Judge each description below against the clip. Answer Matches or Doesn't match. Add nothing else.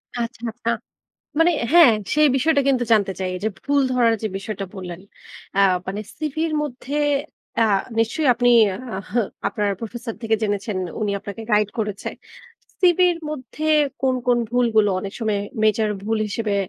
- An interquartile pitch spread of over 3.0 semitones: Matches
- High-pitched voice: Matches